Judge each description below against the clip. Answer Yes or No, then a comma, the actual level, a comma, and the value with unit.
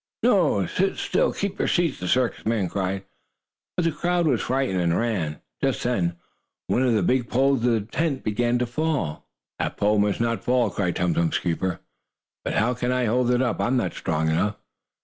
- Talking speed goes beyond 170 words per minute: Yes, fast, 205 wpm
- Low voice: Yes, low, 120 Hz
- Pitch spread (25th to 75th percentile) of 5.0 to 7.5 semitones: Yes, wide, 5.4 semitones